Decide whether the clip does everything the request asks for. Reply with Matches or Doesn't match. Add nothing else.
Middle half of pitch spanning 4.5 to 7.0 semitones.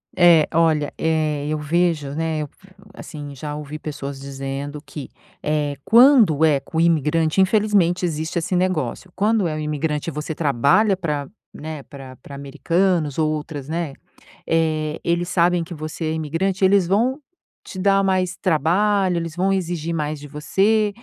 Doesn't match